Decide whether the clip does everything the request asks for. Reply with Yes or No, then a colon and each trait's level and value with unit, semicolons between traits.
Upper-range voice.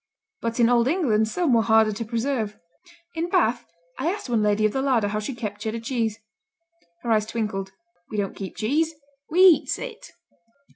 Yes: high, 230 Hz